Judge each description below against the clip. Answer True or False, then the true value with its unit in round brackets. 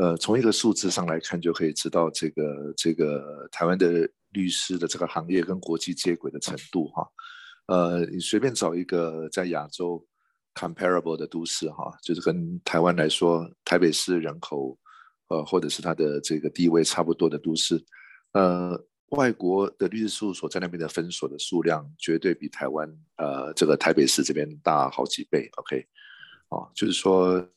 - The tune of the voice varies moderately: False (2.1 semitones)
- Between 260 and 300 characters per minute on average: True (290 characters per minute)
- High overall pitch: False (85 Hz)